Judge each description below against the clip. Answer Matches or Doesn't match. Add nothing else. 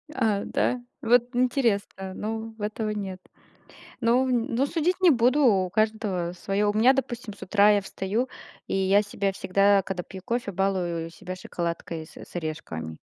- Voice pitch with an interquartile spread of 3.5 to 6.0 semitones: Matches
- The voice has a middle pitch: Doesn't match